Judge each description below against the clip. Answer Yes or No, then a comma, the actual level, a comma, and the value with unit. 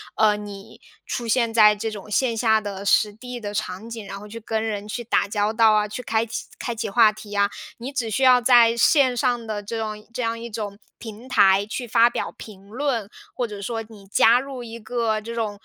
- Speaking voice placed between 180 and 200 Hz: No, high, 220 Hz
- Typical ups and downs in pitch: No, narrow, 2.1 semitones